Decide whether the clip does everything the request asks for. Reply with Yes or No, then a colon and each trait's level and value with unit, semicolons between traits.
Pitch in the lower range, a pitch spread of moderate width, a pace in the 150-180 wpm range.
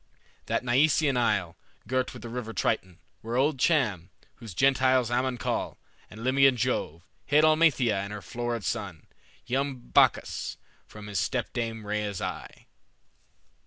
No: low, 120 Hz; average, 3.9 semitones; slow, 135 wpm